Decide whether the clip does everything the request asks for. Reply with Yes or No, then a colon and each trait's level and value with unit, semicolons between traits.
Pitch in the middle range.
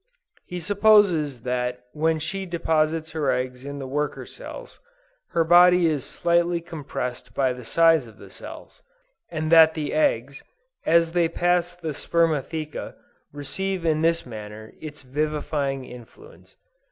Yes: medium, 155 Hz